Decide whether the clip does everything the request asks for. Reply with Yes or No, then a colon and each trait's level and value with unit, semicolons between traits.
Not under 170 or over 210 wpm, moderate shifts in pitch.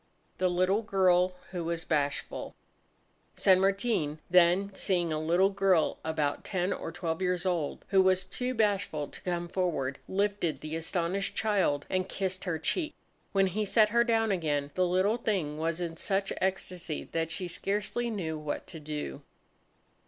No: average, 160 wpm; average, 3.2 semitones